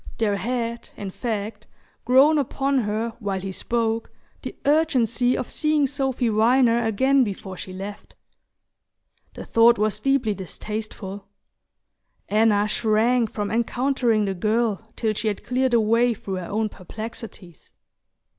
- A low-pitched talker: No, high, 225 Hz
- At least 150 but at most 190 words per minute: No, slow, 135 wpm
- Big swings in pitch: No, average, 3.0 semitones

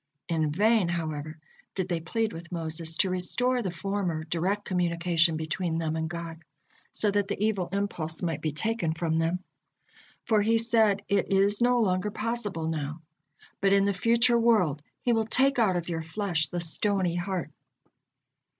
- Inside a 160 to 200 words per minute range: Yes, average, 170 wpm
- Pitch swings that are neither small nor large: Yes, average, 4.2 semitones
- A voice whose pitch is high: No, medium, 180 Hz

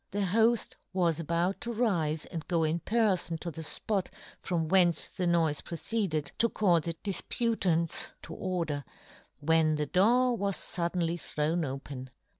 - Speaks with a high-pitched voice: No, medium, 170 Hz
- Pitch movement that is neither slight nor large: Yes, average, 3.6 semitones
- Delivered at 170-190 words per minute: No, average, 155 wpm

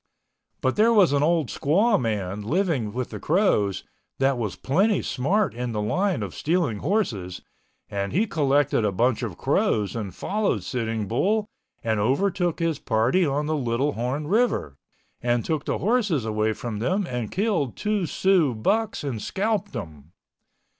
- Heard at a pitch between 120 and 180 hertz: Yes, low, 135 Hz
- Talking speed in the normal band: Yes, average, 160 wpm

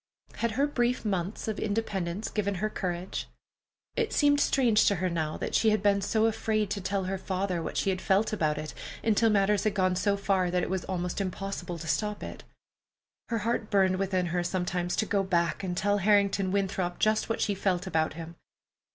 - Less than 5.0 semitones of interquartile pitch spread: Yes, average, 2.8 semitones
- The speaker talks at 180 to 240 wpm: Yes, average, 200 wpm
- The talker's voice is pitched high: Yes, high, 195 Hz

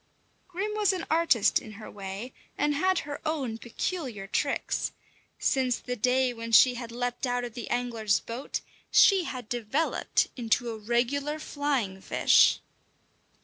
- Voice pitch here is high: Yes, high, 245 Hz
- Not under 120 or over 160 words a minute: Yes, average, 145 wpm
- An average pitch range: Yes, average, 4.3 semitones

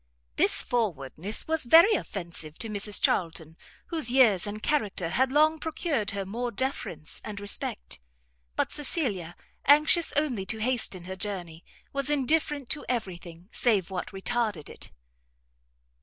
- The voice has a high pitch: Yes, high, 215 Hz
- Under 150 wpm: Yes, average, 140 wpm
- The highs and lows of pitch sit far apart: Yes, wide, 7.1 semitones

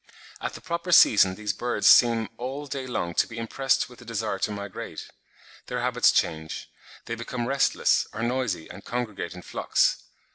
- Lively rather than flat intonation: No, average, 3.6 semitones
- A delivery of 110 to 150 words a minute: No, average, 175 wpm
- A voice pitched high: No, low, 115 Hz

